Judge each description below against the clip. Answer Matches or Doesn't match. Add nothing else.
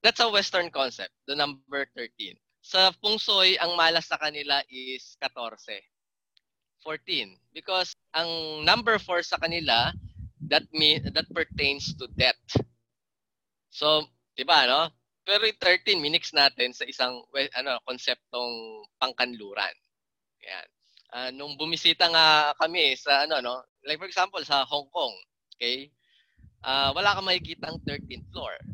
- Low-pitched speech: Doesn't match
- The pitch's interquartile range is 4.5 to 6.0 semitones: Matches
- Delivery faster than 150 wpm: Doesn't match